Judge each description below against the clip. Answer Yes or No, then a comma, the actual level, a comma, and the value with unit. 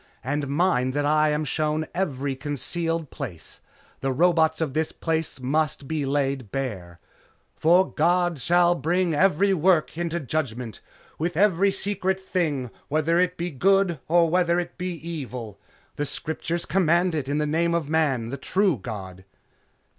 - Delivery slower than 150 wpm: No, average, 155 wpm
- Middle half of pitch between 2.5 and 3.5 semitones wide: No, average, 4.1 semitones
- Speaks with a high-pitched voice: No, medium, 155 Hz